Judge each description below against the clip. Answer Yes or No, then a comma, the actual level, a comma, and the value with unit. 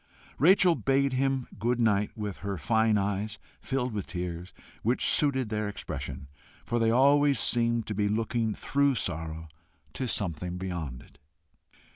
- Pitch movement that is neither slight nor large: Yes, average, 4.8 semitones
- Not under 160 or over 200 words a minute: No, average, 145 wpm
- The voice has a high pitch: No, low, 110 Hz